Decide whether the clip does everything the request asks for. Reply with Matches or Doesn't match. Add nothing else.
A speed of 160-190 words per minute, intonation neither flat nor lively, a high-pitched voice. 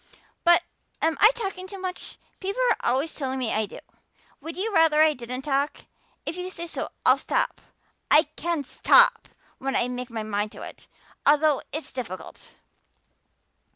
Doesn't match